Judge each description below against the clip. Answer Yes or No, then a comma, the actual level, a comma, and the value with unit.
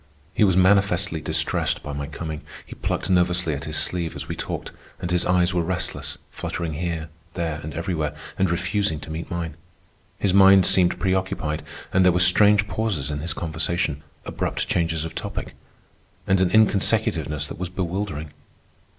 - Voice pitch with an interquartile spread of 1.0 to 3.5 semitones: Yes, average, 3.0 semitones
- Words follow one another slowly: No, average, 165 wpm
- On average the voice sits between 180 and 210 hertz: No, very low, 85 Hz